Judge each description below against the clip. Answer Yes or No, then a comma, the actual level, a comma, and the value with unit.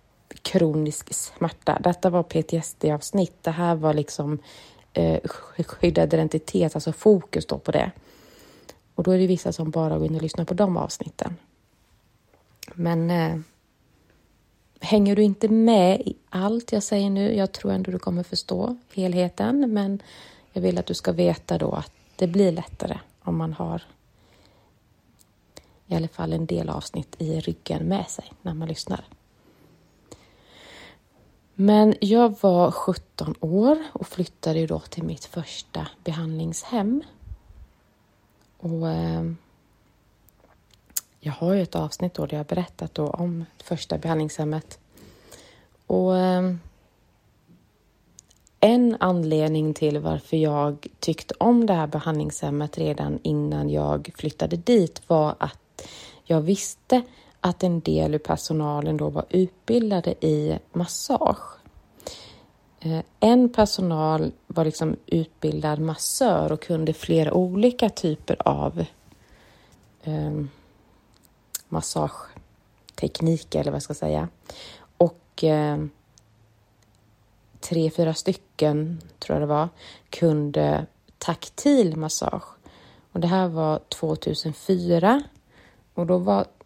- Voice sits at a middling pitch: Yes, medium, 160 Hz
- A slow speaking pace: Yes, slow, 120 wpm